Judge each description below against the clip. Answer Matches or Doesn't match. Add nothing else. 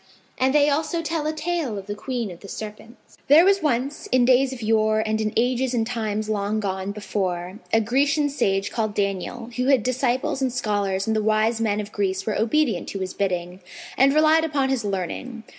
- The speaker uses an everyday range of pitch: Matches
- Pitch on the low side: Doesn't match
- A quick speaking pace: Matches